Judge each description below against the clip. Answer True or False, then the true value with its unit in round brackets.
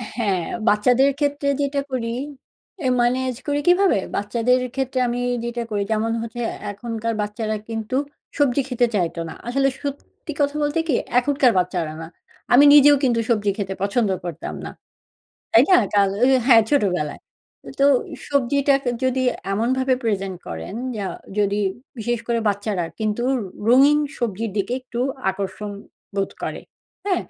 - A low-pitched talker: False (235 Hz)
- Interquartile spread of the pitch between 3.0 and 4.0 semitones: False (4.5 semitones)